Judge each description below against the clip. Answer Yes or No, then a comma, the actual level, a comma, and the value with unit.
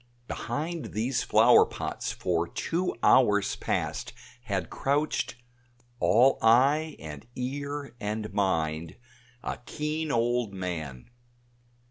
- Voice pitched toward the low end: Yes, low, 115 Hz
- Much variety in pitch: Yes, wide, 7.3 semitones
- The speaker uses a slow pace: Yes, slow, 100 wpm